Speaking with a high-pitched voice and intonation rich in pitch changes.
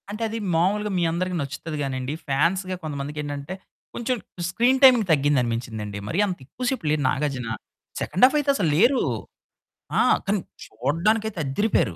No: medium, 165 Hz; wide, 7.1 semitones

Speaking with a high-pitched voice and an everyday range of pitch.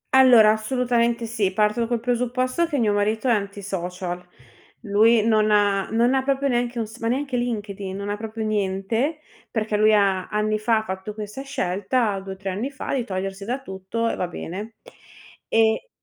Yes: high, 220 Hz; average, 3.2 semitones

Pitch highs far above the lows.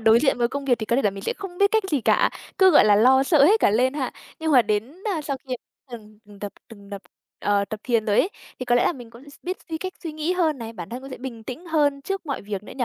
Yes: wide, 6.0 semitones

